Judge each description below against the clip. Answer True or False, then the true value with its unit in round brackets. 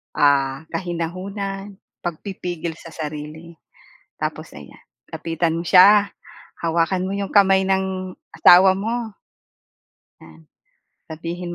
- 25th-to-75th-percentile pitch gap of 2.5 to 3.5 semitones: True (2.9 semitones)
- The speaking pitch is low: False (180 Hz)